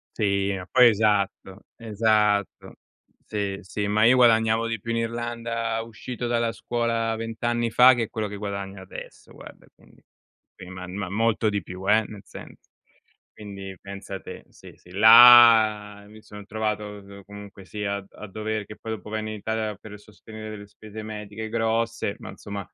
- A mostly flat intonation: Yes, narrow, 2.1 semitones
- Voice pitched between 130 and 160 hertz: No, low, 105 Hz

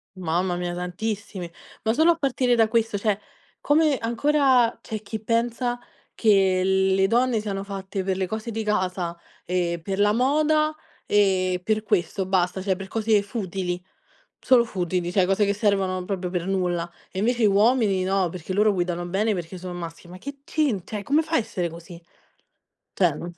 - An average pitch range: Yes, average, 3.7 semitones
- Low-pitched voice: No, high, 195 Hz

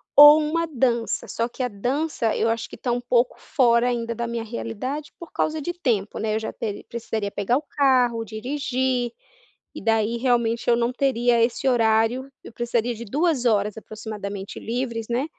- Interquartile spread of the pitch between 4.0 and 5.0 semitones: No, narrow, 2.5 semitones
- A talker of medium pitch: No, high, 235 Hz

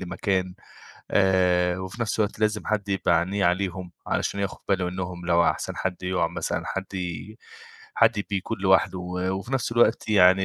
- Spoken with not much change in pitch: Yes, narrow, 2.0 semitones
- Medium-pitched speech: No, very low, 95 Hz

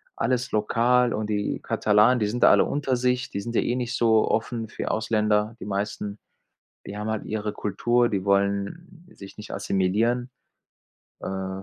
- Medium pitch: No, low, 110 Hz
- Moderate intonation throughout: Yes, average, 3.0 semitones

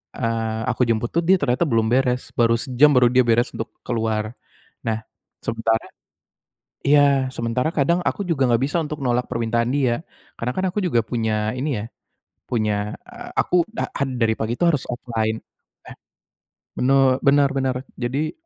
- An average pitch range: Yes, average, 3.4 semitones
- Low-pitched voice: Yes, low, 125 Hz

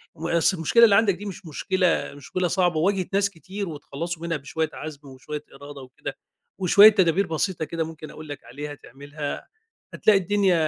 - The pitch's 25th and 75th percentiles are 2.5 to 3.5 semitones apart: No, average, 4.3 semitones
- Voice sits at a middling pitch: Yes, medium, 165 Hz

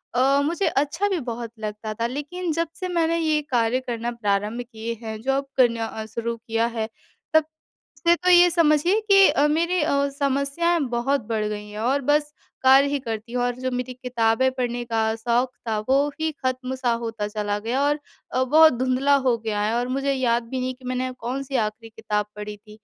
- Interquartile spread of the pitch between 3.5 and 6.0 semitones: Yes, average, 3.9 semitones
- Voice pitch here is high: Yes, very high, 255 Hz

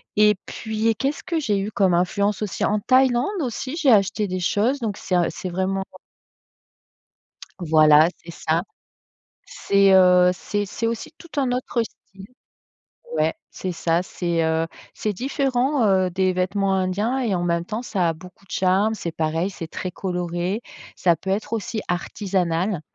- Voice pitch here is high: Yes, high, 195 Hz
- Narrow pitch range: No, average, 3.7 semitones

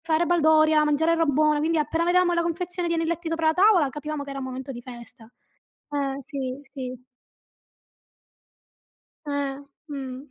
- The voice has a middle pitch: No, very high, 305 Hz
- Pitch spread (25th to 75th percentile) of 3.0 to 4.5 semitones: Yes, average, 3.4 semitones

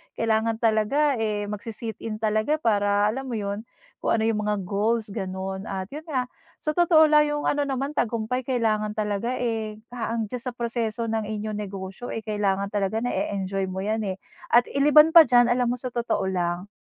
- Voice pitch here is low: No, high, 220 Hz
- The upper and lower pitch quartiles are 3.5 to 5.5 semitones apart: No, average, 3.1 semitones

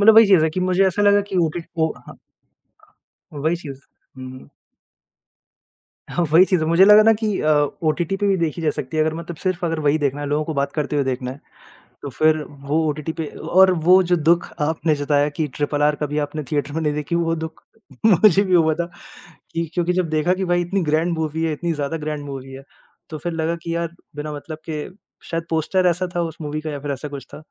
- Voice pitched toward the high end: No, medium, 160 Hz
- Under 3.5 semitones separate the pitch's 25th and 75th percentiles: Yes, average, 2.8 semitones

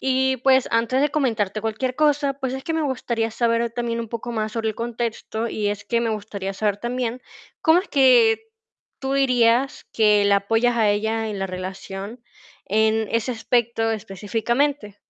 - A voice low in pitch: No, high, 230 Hz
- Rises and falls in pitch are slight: No, average, 3.0 semitones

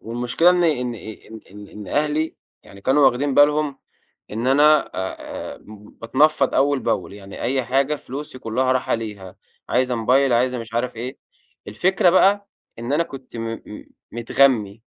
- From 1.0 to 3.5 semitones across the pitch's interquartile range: No, average, 4.2 semitones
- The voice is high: No, low, 125 Hz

